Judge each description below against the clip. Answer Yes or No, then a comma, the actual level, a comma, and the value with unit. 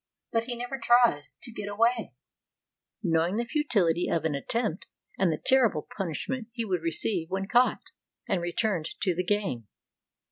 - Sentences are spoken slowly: No, average, 155 wpm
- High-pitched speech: Yes, high, 200 Hz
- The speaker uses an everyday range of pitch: No, wide, 5.8 semitones